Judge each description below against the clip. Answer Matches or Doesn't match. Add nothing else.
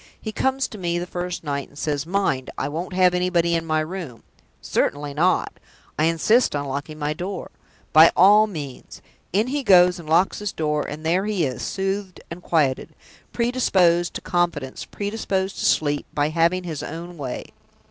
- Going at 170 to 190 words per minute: Matches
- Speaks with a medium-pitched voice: Matches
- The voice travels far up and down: Doesn't match